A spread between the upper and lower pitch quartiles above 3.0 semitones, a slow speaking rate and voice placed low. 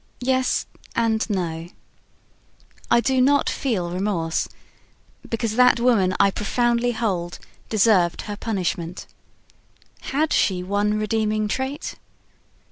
No: average, 4.5 semitones; slow, 105 wpm; high, 215 Hz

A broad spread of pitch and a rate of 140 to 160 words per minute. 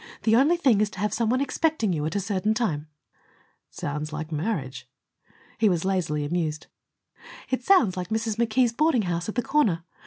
No: wide, 6.5 semitones; average, 190 wpm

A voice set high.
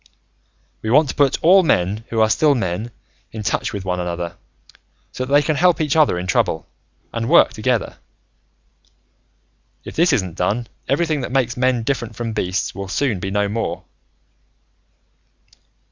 No: low, 115 Hz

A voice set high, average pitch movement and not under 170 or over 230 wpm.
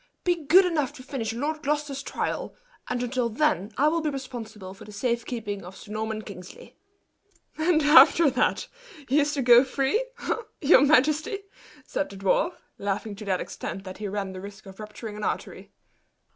No: very high, 250 Hz; wide, 6.1 semitones; average, 180 wpm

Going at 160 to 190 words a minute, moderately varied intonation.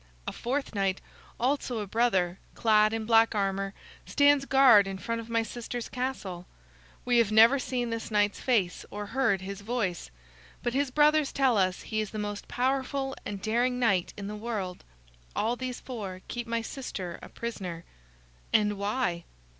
Yes: average, 170 wpm; average, 3.9 semitones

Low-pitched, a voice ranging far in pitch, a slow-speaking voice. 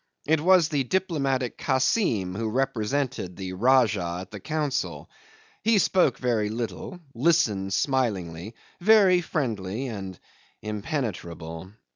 Yes: low, 120 Hz; wide, 7.3 semitones; slow, 110 wpm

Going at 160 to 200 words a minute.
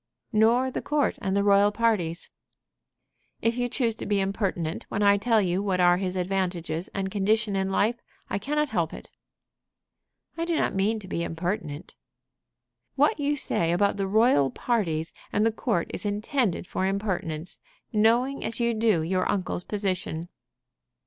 Yes: average, 165 wpm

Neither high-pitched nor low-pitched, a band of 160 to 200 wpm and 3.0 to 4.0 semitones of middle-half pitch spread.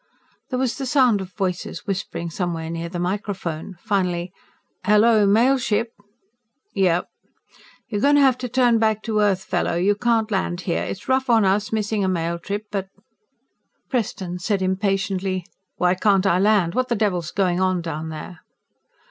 No: high, 195 Hz; average, 170 wpm; average, 3.6 semitones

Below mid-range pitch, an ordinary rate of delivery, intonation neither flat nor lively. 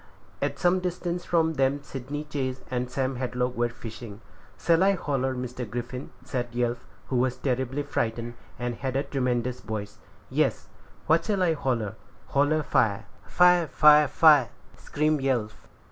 Yes: low, 130 Hz; average, 150 wpm; average, 3.7 semitones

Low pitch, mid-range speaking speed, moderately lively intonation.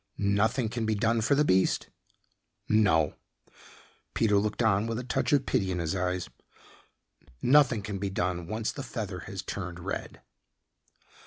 Yes: low, 105 Hz; average, 155 wpm; average, 3.7 semitones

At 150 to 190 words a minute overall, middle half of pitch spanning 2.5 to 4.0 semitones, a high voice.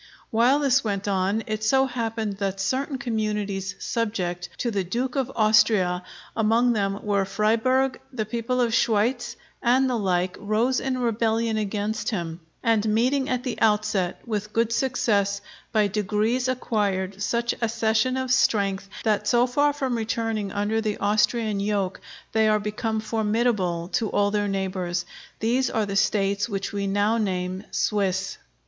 Yes: average, 155 wpm; average, 2.9 semitones; high, 215 Hz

